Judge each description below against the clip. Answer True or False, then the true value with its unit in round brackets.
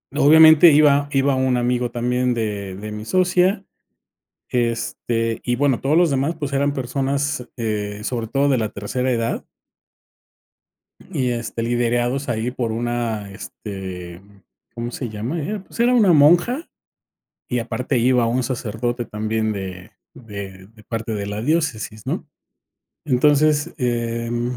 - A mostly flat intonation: False (4.1 semitones)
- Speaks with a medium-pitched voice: False (120 Hz)